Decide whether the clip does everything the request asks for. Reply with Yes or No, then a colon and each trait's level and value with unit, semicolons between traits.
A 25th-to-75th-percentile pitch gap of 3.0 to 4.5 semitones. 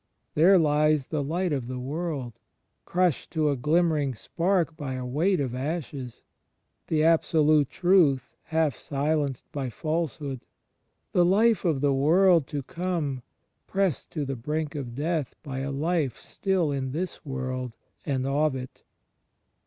Yes: average, 3.8 semitones